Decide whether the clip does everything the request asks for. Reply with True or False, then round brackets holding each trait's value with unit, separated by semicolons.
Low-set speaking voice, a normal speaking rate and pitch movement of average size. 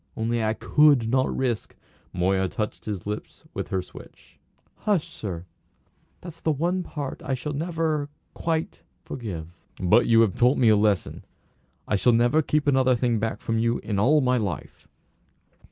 False (120 Hz; 170 wpm; 5.7 semitones)